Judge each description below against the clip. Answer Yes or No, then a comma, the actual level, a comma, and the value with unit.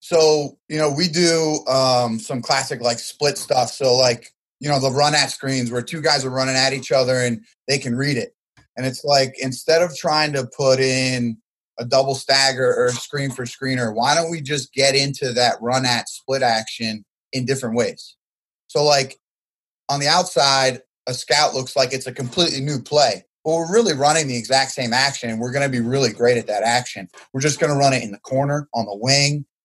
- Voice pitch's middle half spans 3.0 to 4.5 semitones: No, narrow, 2.6 semitones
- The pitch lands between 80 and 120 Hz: No, low, 135 Hz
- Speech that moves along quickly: Yes, fast, 215 wpm